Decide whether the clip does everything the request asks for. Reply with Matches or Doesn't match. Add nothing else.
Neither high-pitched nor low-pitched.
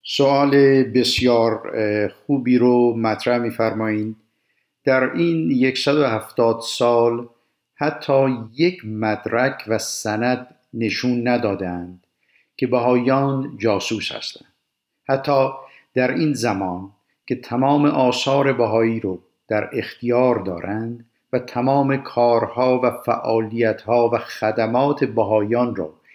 Doesn't match